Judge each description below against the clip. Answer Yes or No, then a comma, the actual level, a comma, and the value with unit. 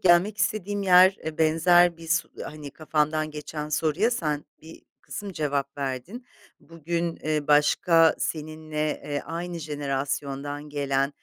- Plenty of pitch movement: No, average, 2.8 semitones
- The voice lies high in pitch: No, medium, 155 Hz